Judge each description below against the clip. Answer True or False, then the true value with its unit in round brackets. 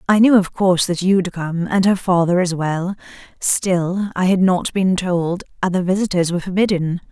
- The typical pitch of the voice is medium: True (180 Hz)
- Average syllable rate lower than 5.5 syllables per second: True (4.8 syllables/s)